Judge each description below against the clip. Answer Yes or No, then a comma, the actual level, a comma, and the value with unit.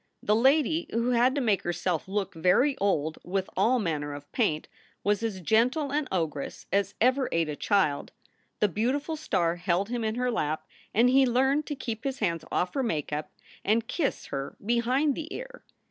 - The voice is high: Yes, high, 220 Hz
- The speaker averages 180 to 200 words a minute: Yes, average, 190 wpm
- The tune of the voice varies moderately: No, wide, 6.9 semitones